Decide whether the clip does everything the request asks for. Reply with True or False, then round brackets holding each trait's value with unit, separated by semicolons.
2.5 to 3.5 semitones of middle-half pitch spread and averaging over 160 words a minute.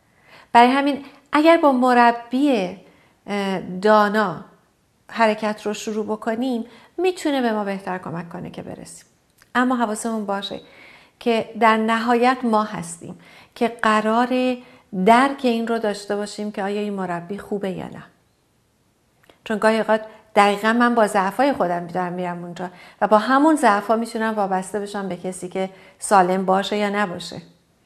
False (3.2 semitones; 140 wpm)